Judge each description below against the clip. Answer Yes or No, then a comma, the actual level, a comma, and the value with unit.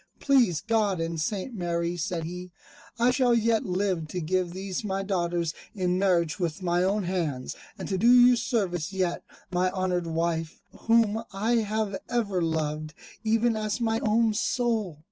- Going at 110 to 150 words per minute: No, average, 165 wpm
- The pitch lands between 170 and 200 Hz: Yes, high, 190 Hz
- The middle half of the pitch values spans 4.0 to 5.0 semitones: Yes, average, 4.4 semitones